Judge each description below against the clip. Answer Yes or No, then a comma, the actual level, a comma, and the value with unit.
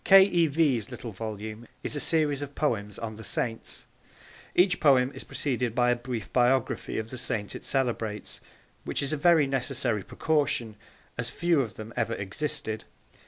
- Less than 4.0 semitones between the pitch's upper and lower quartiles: No, average, 4.7 semitones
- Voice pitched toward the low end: Yes, low, 125 Hz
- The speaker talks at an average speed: Yes, average, 170 wpm